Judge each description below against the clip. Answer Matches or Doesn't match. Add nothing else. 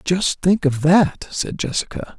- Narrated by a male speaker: Matches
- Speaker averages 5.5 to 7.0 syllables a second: Doesn't match